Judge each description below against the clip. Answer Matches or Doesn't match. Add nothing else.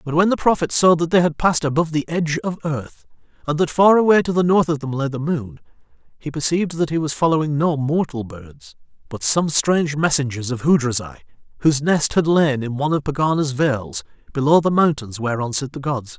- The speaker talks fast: Matches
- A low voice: Doesn't match